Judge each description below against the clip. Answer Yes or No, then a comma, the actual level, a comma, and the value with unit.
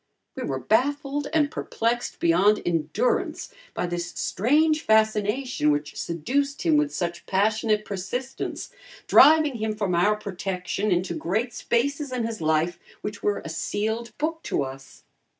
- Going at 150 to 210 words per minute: No, average, 140 wpm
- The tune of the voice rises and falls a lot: Yes, wide, 7.3 semitones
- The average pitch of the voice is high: Yes, high, 215 Hz